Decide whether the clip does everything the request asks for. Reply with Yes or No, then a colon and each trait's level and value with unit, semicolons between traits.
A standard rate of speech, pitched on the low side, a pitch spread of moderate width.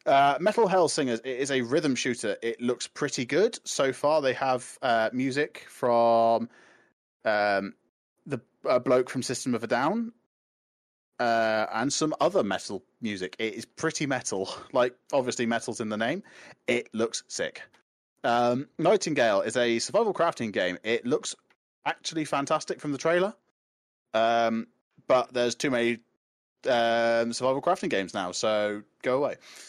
Yes: average, 150 wpm; low, 120 Hz; average, 3.0 semitones